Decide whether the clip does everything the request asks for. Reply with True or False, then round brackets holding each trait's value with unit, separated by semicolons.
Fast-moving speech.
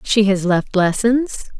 False (150 wpm)